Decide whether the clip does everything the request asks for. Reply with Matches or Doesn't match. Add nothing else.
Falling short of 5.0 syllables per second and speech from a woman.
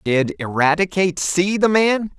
Doesn't match